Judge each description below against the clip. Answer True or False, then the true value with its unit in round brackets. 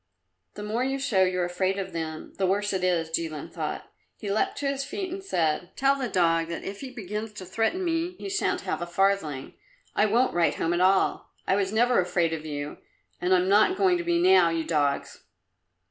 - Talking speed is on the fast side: True (215 wpm)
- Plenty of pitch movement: True (6.9 semitones)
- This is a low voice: False (195 Hz)